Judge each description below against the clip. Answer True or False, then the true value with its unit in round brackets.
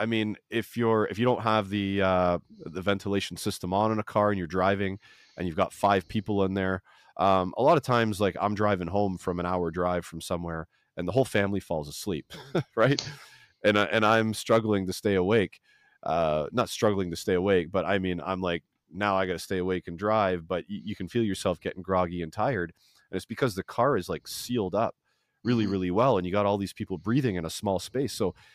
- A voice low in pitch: True (100 Hz)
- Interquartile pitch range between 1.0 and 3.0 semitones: True (2.7 semitones)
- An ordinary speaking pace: False (230 wpm)